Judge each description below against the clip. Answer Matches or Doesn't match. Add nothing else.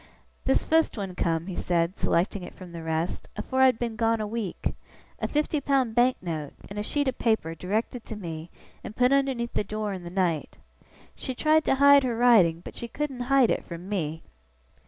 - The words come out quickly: Matches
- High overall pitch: Matches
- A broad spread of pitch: Matches